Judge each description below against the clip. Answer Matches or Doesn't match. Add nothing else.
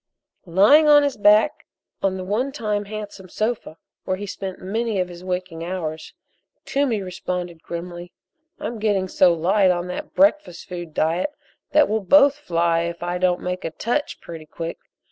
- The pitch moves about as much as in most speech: Matches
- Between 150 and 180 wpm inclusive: Matches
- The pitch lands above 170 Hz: Matches